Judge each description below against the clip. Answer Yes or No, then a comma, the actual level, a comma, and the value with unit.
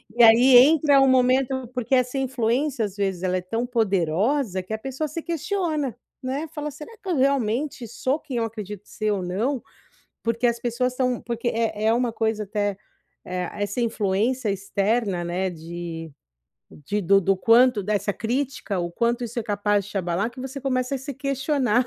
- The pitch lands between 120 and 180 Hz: No, high, 235 Hz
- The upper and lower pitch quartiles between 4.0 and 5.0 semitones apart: Yes, average, 4.5 semitones